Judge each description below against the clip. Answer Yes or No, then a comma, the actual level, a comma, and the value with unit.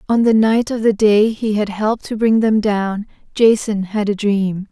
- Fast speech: Yes, fast, 215 wpm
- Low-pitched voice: No, high, 210 Hz